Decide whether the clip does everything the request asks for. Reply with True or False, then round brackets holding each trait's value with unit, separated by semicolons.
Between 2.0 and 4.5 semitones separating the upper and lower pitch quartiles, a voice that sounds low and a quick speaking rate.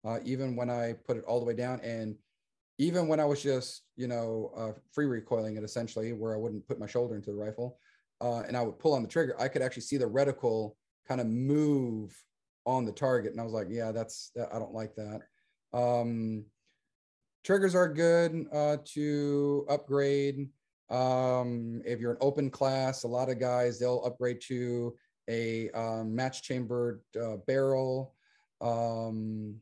False (2.9 semitones; 120 Hz; 180 wpm)